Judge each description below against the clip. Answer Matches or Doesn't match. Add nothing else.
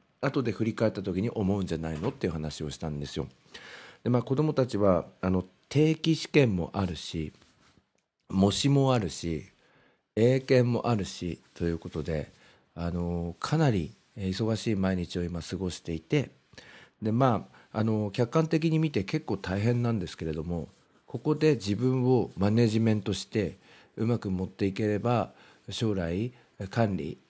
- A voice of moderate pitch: Doesn't match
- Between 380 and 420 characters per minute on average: Doesn't match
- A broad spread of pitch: Matches